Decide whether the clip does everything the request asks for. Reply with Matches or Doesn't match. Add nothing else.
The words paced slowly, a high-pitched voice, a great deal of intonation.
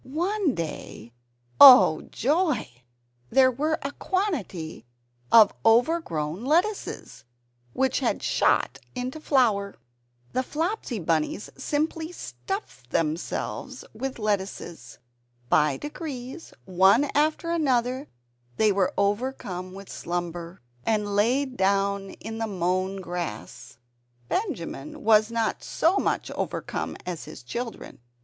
Matches